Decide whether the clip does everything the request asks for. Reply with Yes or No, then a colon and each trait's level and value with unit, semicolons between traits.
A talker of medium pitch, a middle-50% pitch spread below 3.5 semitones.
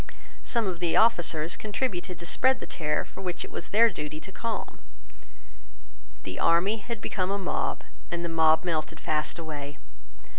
No: medium, 175 Hz; average, 4.4 semitones